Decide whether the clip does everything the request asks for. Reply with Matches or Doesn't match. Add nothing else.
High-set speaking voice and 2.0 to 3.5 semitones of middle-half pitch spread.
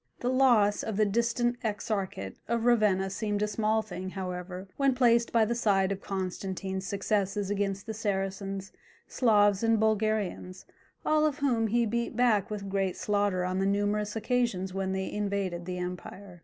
Matches